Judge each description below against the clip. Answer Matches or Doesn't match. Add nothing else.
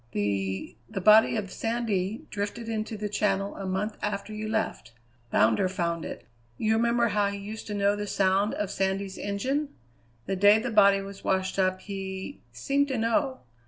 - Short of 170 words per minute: Doesn't match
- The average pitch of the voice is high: Matches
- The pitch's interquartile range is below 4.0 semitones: Matches